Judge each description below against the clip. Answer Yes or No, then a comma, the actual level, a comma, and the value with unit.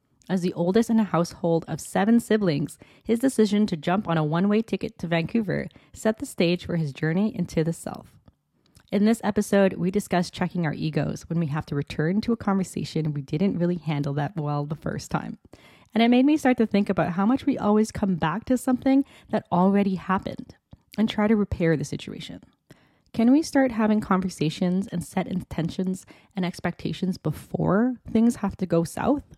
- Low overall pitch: No, high, 190 Hz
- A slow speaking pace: No, average, 195 wpm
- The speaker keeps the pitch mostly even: No, average, 4.6 semitones